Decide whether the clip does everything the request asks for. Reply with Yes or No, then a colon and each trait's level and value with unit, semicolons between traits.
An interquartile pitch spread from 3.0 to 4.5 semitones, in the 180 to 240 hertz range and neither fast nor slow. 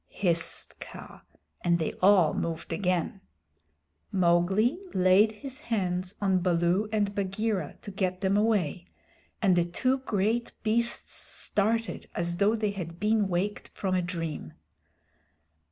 No: average, 3.4 semitones; high, 190 Hz; slow, 130 wpm